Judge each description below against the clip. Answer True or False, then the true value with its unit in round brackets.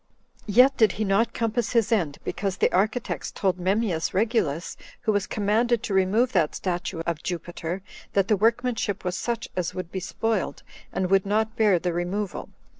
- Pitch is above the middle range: True (200 Hz)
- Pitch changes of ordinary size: True (3.7 semitones)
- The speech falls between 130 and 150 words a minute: False (175 wpm)